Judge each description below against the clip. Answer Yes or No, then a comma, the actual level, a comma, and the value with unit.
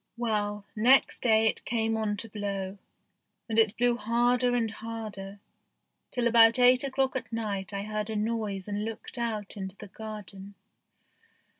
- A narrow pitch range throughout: Yes, narrow, 2.3 semitones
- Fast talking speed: No, average, 155 wpm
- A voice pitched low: No, high, 220 Hz